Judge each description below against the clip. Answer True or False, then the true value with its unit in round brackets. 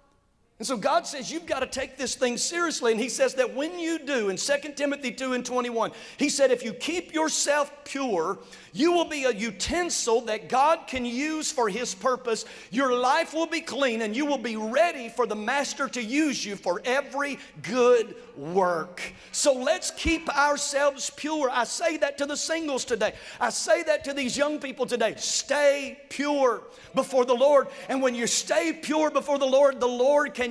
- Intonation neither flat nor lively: True (3.1 semitones)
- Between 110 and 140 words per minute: False (195 wpm)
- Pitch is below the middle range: False (270 Hz)